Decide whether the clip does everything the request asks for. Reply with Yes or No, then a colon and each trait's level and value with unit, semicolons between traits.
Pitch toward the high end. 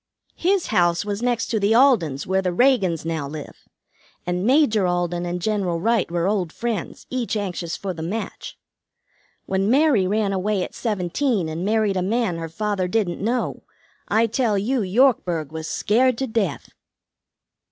Yes: high, 200 Hz